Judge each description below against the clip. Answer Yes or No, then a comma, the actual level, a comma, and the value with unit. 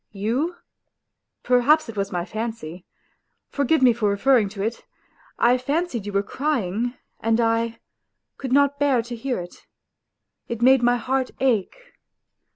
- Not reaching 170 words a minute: Yes, average, 145 wpm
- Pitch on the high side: Yes, high, 240 Hz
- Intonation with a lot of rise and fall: No, average, 3.9 semitones